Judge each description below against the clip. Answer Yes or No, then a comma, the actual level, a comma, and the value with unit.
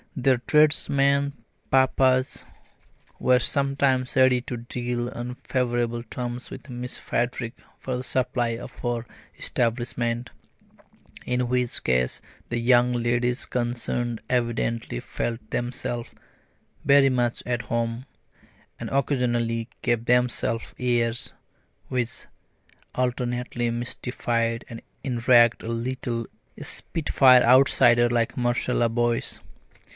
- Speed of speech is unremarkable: No, slow, 100 wpm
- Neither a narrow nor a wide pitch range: No, narrow, 1.3 semitones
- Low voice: Yes, low, 120 Hz